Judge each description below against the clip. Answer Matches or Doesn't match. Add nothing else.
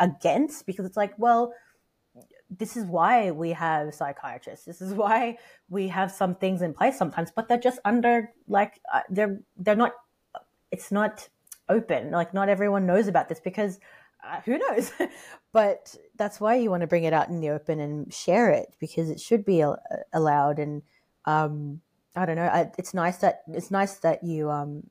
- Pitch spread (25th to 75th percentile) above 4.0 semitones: Matches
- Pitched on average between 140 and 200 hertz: Matches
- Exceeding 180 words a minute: Matches